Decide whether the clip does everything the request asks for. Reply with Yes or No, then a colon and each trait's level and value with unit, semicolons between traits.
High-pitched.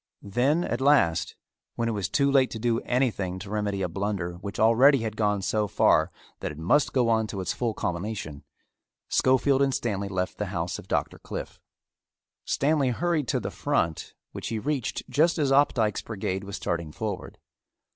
No: low, 110 Hz